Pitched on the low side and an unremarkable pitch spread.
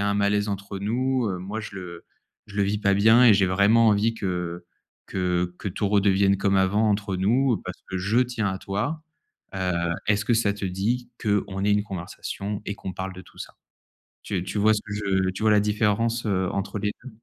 No: low, 100 Hz; narrow, 2.0 semitones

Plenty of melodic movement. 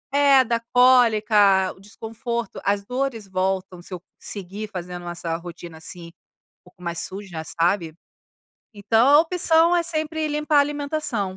Yes: wide, 7.2 semitones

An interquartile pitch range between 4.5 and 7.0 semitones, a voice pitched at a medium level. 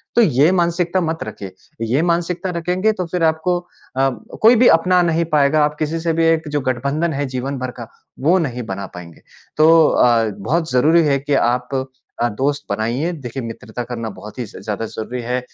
Yes: wide, 5.4 semitones; medium, 145 Hz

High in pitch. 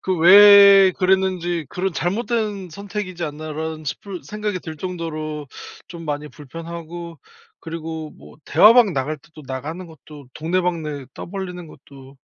No: medium, 170 Hz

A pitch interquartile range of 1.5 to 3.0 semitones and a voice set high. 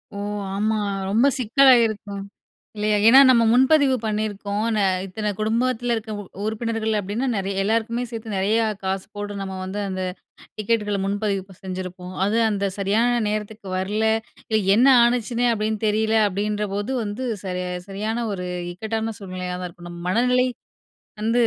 Yes: narrow, 2.5 semitones; high, 215 Hz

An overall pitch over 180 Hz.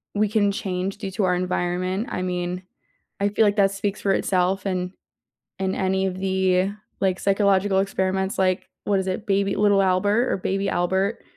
Yes: high, 190 Hz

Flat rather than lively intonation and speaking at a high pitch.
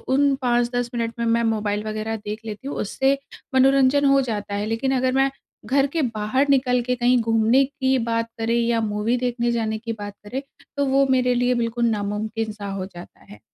No: average, 3.1 semitones; high, 235 Hz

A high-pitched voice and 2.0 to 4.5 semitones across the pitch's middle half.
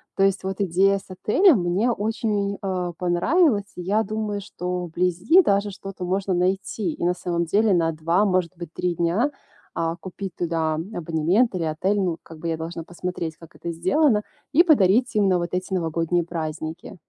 No: medium, 180 Hz; average, 3.0 semitones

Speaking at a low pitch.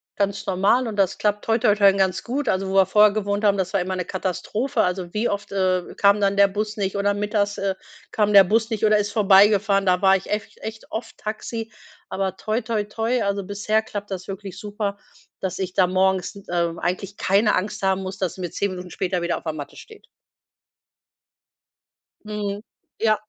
No: high, 200 Hz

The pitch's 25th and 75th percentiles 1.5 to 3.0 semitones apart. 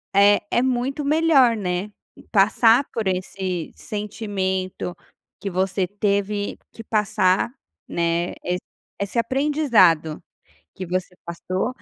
No: average, 3.8 semitones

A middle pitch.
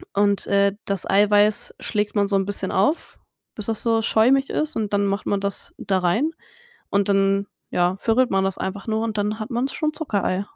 No: high, 205 Hz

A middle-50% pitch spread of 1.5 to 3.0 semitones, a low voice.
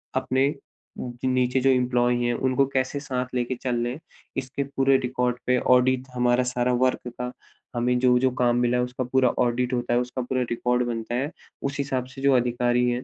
No: narrow, 1.1 semitones; low, 125 Hz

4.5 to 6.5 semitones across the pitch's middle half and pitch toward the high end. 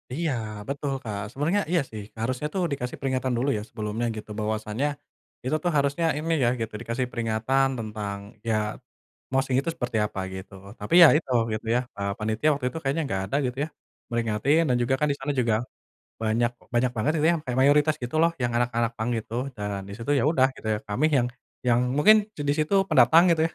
No: average, 4.8 semitones; low, 125 Hz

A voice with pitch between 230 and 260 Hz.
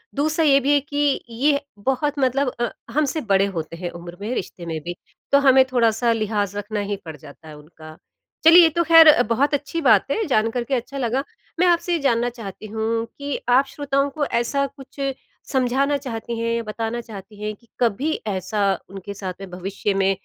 Yes: high, 235 Hz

